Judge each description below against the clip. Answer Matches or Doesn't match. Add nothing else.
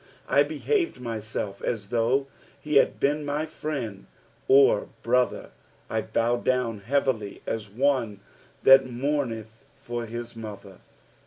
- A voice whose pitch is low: Matches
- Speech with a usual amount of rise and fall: Matches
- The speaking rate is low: Matches